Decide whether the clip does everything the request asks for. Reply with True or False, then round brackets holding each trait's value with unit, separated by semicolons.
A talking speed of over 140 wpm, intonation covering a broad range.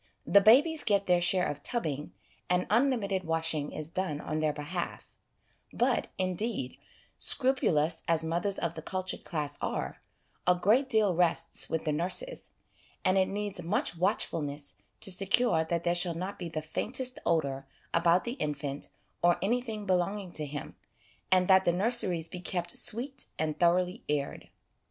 False (155 wpm; 3.9 semitones)